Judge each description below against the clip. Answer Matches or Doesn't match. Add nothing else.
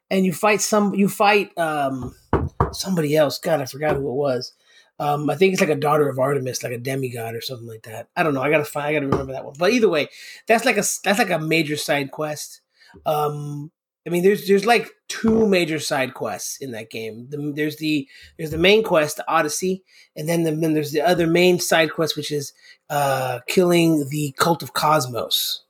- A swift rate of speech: Matches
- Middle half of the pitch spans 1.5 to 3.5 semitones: Doesn't match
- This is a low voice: Doesn't match